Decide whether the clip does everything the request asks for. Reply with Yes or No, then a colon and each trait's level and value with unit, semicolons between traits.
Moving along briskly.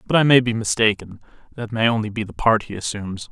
Yes: fast, 235 wpm